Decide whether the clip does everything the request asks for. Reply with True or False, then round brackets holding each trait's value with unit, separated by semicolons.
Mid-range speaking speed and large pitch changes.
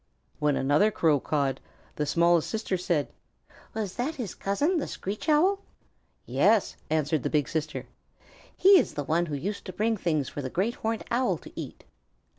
True (175 wpm; 7.0 semitones)